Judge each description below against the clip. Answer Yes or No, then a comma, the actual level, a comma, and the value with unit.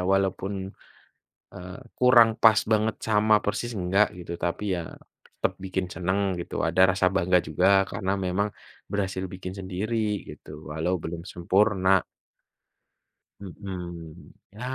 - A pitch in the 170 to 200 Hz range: No, very low, 95 Hz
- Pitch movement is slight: Yes, narrow, 2.2 semitones